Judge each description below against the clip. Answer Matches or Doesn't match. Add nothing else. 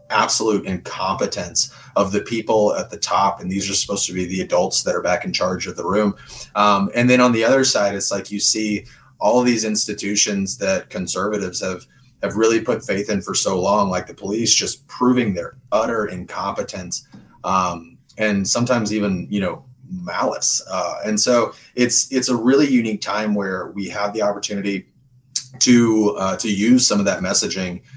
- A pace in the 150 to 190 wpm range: Matches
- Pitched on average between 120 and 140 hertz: Doesn't match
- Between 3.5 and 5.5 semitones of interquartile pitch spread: Matches